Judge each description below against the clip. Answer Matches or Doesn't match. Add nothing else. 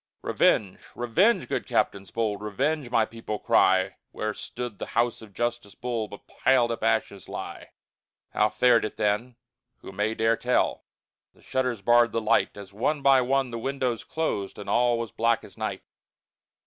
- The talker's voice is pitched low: Matches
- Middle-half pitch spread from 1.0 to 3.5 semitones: Matches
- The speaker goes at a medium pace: Matches